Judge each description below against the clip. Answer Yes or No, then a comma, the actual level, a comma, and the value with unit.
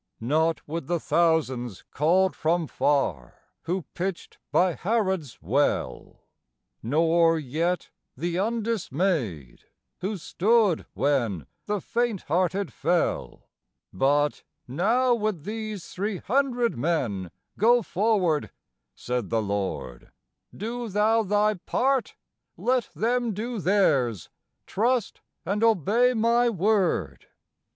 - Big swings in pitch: Yes, wide, 7.0 semitones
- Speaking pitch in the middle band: Yes, medium, 180 Hz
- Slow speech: Yes, slow, 105 wpm